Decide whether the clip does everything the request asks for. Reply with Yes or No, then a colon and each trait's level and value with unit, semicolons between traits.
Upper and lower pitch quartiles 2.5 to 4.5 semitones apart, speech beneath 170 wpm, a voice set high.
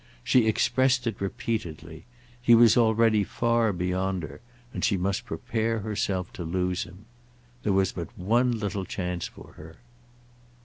No: average, 3.9 semitones; average, 145 wpm; low, 100 Hz